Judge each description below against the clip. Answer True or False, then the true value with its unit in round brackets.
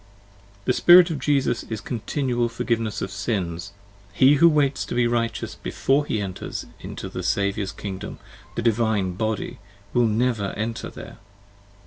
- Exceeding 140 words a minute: True (155 wpm)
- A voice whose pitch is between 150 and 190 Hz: False (115 Hz)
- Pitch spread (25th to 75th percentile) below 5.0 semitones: True (4.1 semitones)